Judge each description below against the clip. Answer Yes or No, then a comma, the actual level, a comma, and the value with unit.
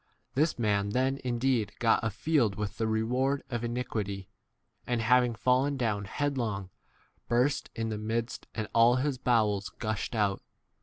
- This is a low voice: Yes, low, 115 Hz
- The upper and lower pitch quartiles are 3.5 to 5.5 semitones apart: No, average, 3.1 semitones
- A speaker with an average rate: Yes, average, 165 wpm